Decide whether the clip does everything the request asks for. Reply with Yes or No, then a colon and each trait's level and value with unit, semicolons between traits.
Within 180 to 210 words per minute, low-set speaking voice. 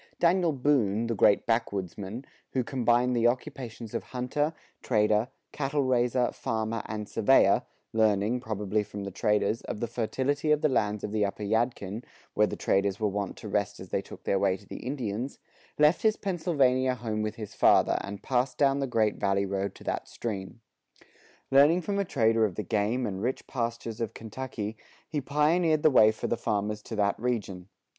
Yes: average, 185 wpm; low, 115 Hz